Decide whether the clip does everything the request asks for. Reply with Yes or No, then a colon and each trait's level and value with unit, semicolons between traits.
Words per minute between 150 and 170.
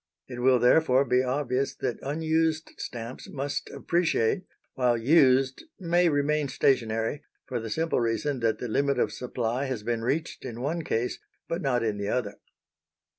Yes: average, 160 wpm